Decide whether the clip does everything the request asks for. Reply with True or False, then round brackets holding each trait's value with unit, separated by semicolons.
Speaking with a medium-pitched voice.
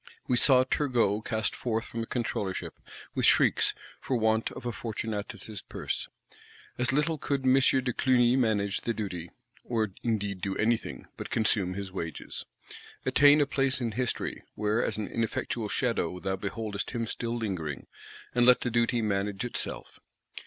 False (115 Hz)